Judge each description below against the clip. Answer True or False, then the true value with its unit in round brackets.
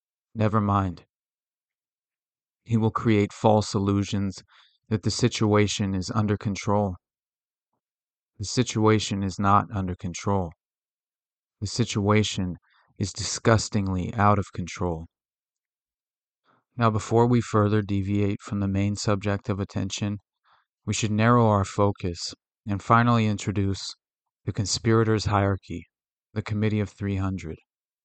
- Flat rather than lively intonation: True (1.9 semitones)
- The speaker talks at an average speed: False (110 wpm)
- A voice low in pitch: True (105 Hz)